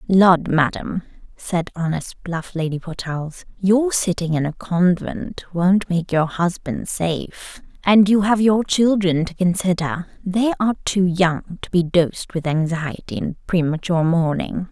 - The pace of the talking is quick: No, average, 145 wpm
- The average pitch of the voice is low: No, medium, 180 Hz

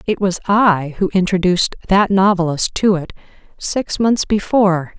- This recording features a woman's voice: Yes, female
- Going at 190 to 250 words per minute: No, average, 145 wpm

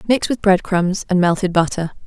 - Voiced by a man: No, female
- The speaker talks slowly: No, fast, 205 wpm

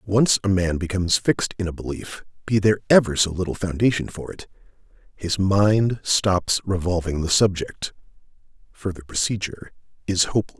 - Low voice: Yes, very low, 95 Hz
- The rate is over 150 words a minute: No, average, 145 wpm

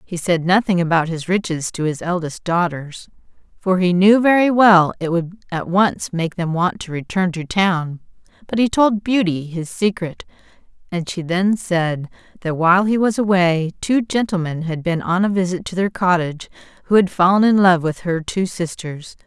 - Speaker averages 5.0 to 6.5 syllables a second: No, 4.7 syllables/s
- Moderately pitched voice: Yes, medium, 180 Hz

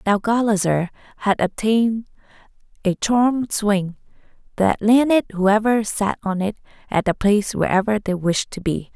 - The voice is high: Yes, high, 205 Hz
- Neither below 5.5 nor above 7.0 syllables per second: No, 4.7 syllables/s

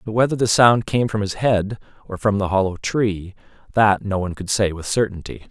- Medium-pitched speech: No, low, 105 Hz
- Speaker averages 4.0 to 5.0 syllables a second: No, 5.3 syllables/s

